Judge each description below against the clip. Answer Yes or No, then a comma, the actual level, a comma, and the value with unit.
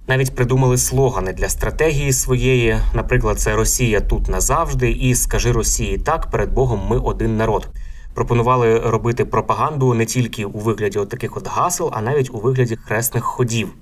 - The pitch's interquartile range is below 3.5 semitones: Yes, average, 2.7 semitones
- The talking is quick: Yes, fast, 160 wpm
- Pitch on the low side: Yes, low, 115 Hz